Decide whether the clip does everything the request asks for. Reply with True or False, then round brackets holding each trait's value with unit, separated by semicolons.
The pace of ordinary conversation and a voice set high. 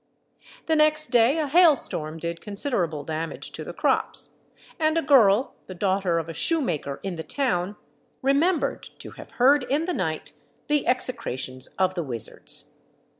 True (160 wpm; 205 Hz)